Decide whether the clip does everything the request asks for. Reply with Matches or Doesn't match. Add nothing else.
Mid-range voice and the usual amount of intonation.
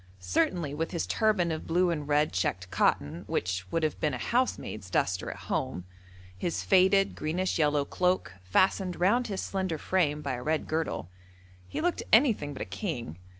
Doesn't match